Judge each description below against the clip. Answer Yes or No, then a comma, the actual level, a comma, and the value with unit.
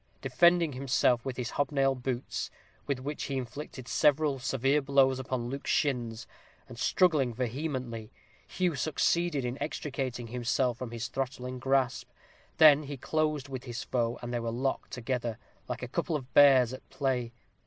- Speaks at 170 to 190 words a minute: No, average, 155 wpm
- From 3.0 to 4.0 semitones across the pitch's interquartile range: No, narrow, 2.6 semitones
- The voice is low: Yes, low, 130 Hz